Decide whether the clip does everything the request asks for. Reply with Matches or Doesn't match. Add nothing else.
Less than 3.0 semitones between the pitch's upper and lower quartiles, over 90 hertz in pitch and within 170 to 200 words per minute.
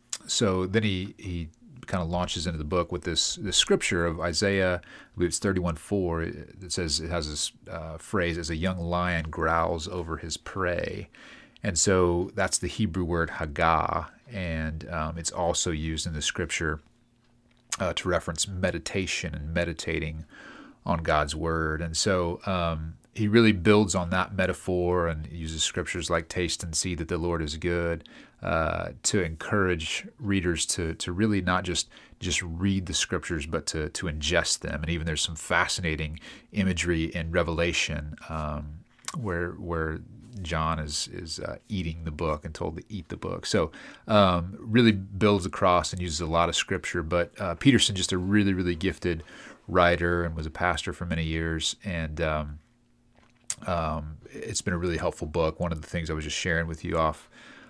Doesn't match